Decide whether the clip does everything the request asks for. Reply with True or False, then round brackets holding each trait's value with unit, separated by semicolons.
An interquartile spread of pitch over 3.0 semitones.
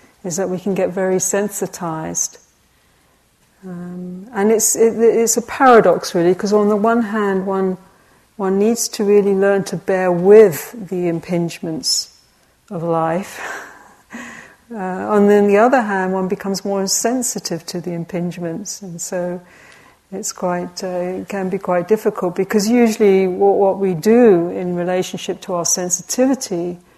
False (2.6 semitones)